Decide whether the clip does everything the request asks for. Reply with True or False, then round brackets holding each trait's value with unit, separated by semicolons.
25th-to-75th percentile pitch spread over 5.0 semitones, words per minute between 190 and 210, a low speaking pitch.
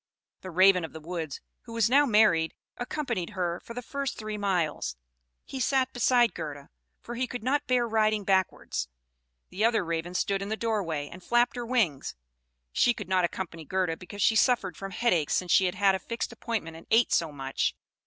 False (5.4 semitones; 195 wpm; 195 Hz)